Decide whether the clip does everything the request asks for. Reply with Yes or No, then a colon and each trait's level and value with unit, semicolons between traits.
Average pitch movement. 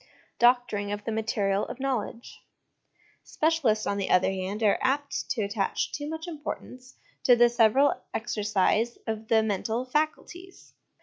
Yes: average, 4.3 semitones